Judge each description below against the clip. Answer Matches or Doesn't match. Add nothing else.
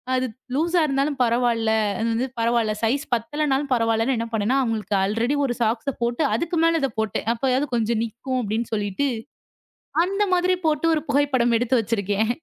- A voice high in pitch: Matches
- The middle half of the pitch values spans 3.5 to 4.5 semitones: Matches